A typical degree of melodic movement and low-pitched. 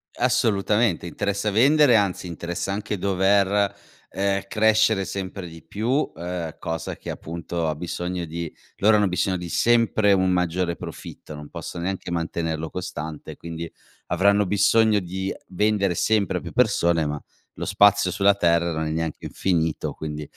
Yes: average, 3.3 semitones; very low, 95 Hz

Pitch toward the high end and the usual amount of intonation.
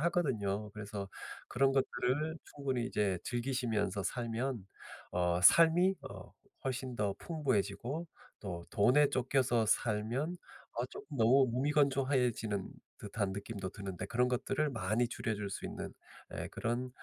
No: low, 120 Hz; average, 4.8 semitones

